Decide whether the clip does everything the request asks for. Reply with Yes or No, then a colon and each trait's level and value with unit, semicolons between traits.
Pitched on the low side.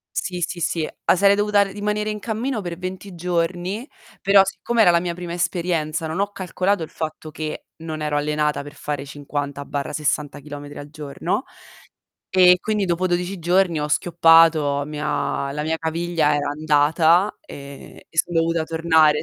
No: medium, 165 Hz